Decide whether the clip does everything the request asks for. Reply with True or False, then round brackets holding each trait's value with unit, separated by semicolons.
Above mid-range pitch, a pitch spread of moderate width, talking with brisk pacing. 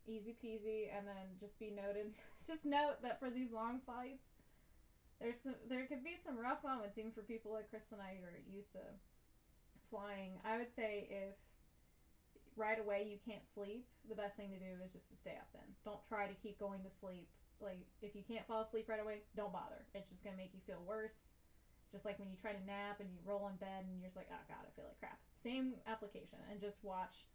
False (210 Hz; 2.1 semitones; 230 wpm)